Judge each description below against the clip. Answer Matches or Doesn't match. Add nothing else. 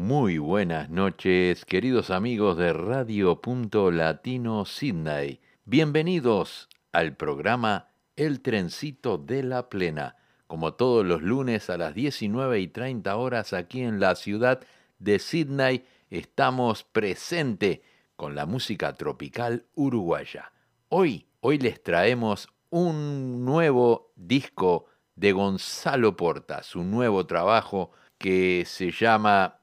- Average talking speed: Doesn't match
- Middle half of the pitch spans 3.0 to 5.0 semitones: Doesn't match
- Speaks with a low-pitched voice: Matches